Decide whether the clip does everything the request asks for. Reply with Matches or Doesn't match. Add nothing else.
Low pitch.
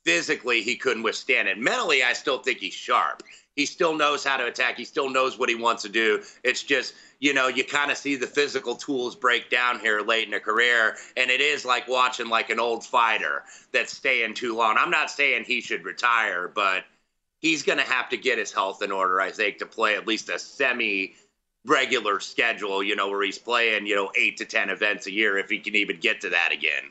Matches